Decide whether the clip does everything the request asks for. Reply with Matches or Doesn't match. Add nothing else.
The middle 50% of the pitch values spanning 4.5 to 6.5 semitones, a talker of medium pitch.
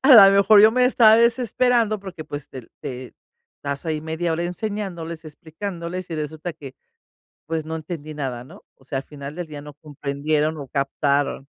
Matches